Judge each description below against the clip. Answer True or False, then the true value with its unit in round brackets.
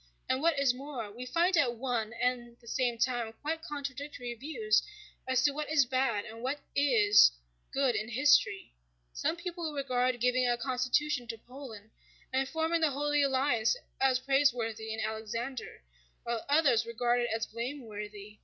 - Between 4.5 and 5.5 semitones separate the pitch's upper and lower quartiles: False (3.6 semitones)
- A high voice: True (250 Hz)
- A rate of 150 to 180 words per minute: True (160 wpm)